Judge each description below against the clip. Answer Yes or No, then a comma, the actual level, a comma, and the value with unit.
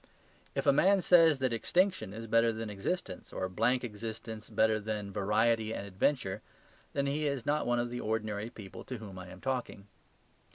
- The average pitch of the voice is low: Yes, low, 115 Hz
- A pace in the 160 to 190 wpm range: Yes, average, 180 wpm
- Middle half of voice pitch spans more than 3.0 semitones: Yes, average, 3.8 semitones